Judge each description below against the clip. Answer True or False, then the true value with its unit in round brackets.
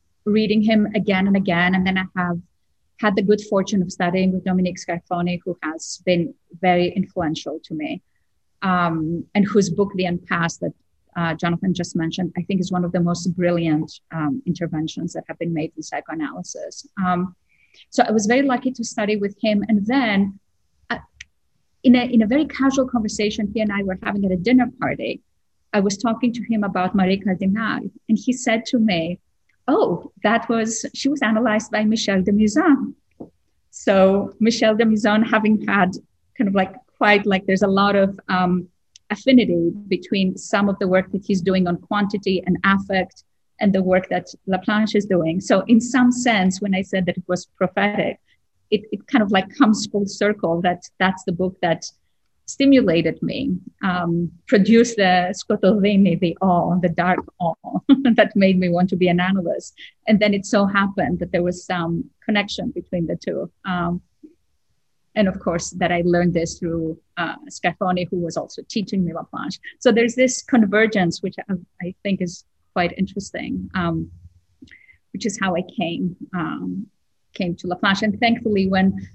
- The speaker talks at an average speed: True (180 wpm)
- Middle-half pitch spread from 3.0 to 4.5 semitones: True (3.3 semitones)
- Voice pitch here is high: True (195 Hz)